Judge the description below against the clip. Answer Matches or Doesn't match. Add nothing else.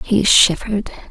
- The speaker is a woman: Matches